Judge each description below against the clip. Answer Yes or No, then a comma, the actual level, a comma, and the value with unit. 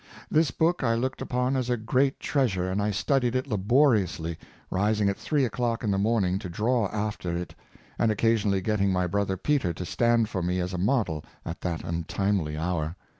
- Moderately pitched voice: No, low, 105 Hz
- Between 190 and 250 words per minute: Yes, average, 195 wpm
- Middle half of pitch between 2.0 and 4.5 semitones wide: No, average, 4.9 semitones